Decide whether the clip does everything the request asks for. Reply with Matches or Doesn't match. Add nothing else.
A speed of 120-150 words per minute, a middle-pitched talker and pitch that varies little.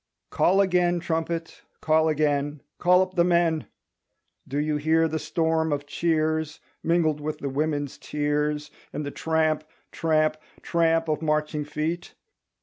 Matches